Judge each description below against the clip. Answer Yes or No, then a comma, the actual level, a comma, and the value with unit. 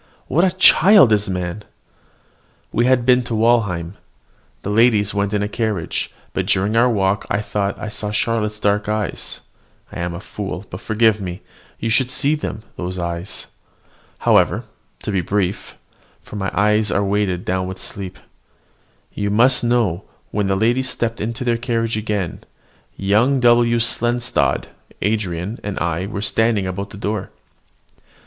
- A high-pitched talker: No, low, 105 Hz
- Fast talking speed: No, average, 160 wpm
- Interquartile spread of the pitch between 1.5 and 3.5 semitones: Yes, average, 3.2 semitones